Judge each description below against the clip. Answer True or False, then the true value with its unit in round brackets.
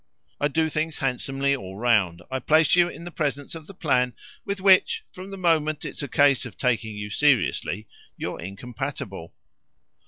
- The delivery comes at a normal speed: True (175 wpm)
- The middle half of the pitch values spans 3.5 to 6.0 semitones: True (5.5 semitones)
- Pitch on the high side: False (140 Hz)